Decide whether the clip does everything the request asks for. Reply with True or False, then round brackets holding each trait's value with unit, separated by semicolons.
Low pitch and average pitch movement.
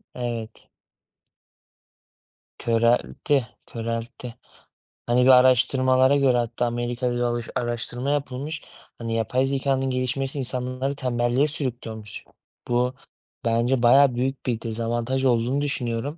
False (125 Hz; 2.0 semitones)